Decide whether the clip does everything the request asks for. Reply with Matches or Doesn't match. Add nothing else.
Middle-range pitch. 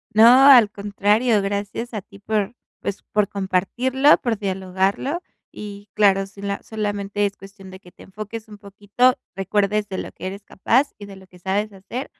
Doesn't match